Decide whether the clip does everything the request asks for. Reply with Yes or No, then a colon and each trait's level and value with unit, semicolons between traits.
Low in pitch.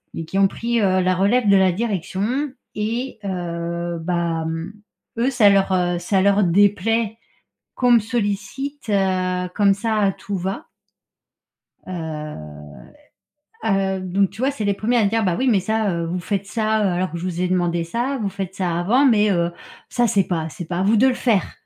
No: high, 195 Hz